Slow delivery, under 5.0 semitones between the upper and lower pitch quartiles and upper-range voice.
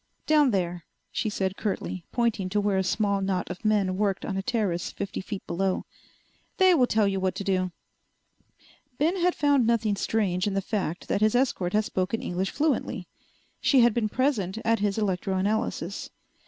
No: average, 180 wpm; average, 3.3 semitones; high, 200 Hz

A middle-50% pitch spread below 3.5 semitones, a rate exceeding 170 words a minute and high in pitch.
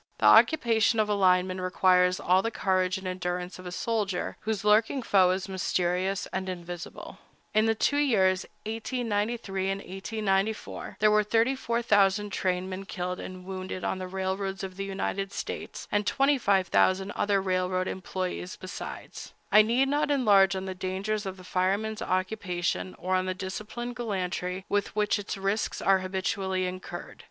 No: narrow, 2.4 semitones; average, 155 wpm; high, 195 Hz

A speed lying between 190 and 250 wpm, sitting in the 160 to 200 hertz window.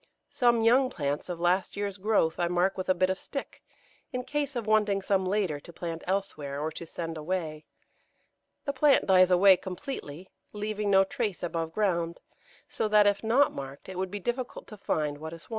Yes: average, 195 wpm; high, 190 Hz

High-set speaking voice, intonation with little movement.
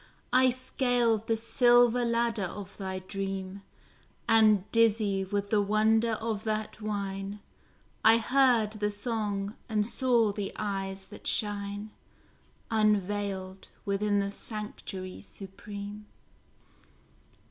Yes: high, 210 Hz; narrow, 2.2 semitones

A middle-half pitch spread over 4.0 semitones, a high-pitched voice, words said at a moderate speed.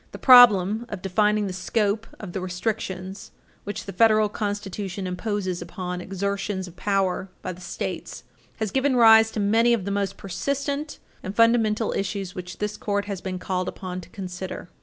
No: average, 2.8 semitones; high, 200 Hz; average, 170 wpm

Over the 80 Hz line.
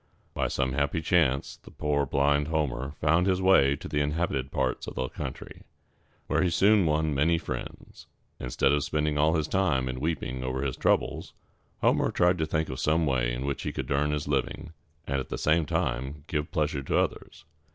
No: very low, 75 Hz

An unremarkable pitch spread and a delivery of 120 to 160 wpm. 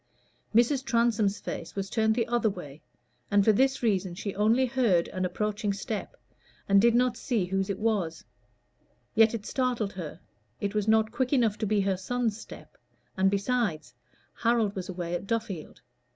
No: average, 3.3 semitones; average, 170 wpm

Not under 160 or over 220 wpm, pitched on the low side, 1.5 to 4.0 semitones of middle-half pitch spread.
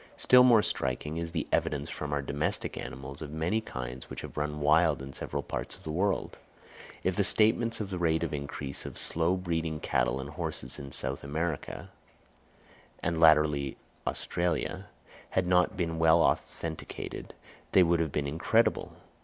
Yes: average, 170 wpm; very low, 80 Hz; average, 3.4 semitones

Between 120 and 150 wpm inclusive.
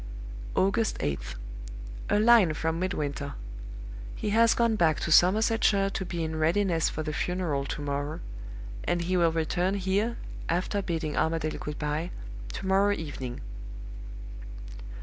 Yes: slow, 135 wpm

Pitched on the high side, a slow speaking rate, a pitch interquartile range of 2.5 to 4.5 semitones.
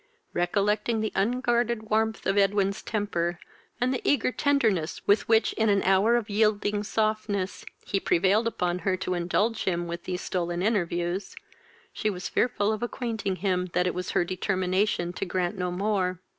No: high, 200 Hz; average, 165 wpm; average, 3.3 semitones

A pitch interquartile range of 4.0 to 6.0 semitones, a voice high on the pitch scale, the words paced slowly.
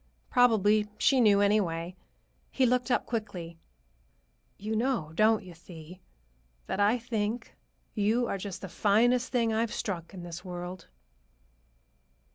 Yes: average, 4.4 semitones; high, 210 Hz; slow, 130 wpm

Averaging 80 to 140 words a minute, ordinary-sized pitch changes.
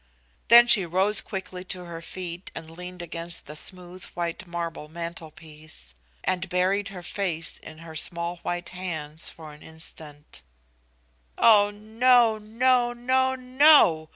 Yes: slow, 135 wpm; average, 4.2 semitones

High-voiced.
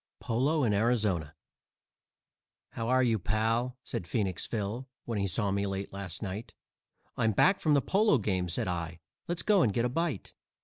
No: low, 110 Hz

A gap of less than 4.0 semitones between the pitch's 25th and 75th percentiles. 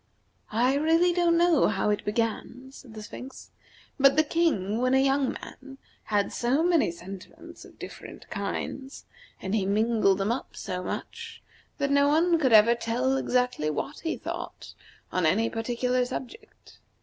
No: average, 5.0 semitones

